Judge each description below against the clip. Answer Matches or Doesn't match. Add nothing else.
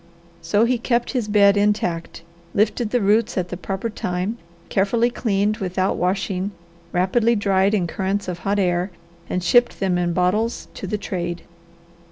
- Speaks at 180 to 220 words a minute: Doesn't match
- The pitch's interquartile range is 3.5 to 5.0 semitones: Doesn't match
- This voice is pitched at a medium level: Doesn't match